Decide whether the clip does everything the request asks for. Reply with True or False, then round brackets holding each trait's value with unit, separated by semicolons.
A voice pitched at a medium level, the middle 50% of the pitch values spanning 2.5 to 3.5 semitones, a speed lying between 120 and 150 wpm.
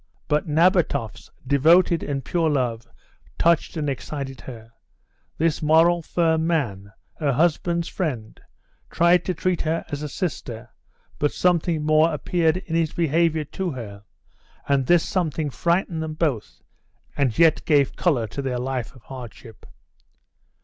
False (155 Hz; 4.1 semitones; 140 wpm)